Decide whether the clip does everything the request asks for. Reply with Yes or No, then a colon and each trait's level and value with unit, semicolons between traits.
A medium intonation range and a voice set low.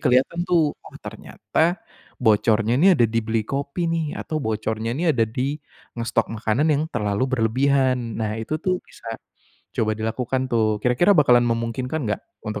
Yes: average, 4.3 semitones; low, 120 Hz